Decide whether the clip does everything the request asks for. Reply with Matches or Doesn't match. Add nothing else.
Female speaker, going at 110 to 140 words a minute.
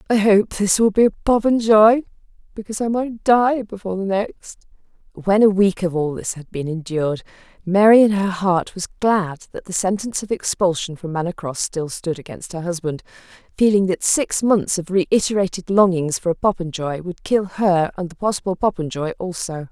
Doesn't match